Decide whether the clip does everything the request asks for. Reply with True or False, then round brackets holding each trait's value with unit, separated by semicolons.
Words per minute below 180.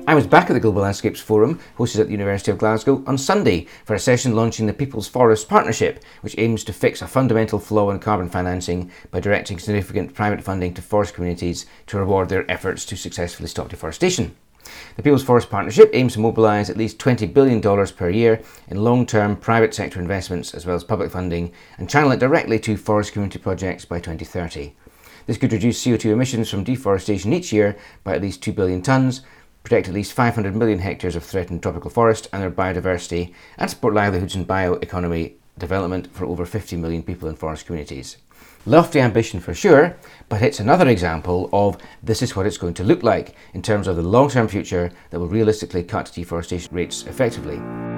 False (195 wpm)